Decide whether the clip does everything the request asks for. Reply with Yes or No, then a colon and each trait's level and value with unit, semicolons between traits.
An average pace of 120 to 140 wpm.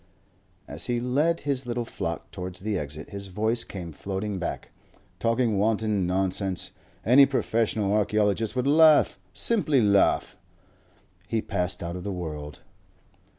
Yes: slow, 135 wpm